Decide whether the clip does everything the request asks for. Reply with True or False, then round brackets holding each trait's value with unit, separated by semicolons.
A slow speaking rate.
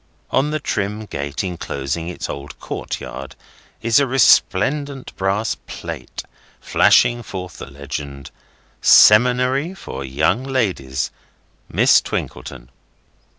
True (105 wpm)